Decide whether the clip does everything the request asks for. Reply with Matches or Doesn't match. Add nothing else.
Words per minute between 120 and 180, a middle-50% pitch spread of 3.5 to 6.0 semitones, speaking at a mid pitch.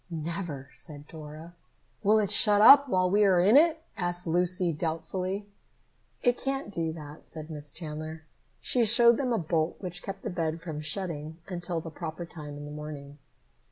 Matches